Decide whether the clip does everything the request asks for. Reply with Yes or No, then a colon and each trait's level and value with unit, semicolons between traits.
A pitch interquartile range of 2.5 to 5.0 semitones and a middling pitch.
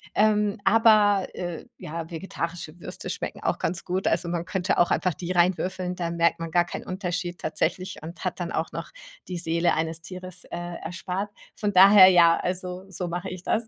No: narrow, 1.8 semitones; medium, 180 Hz